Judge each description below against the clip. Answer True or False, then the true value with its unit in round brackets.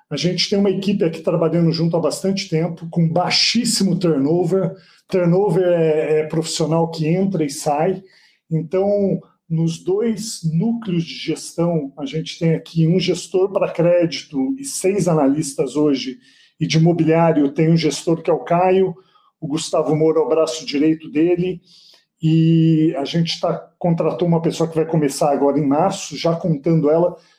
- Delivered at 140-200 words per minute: True (160 wpm)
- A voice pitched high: False (165 Hz)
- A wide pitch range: False (2.4 semitones)